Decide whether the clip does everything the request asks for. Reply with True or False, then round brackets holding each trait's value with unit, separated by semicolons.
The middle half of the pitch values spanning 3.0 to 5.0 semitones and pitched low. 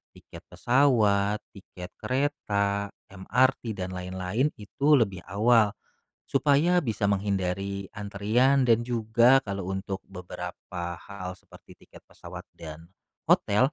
True (4.3 semitones; 100 Hz)